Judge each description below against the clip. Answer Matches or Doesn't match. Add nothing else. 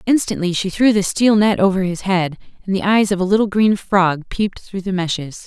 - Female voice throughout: Matches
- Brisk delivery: Matches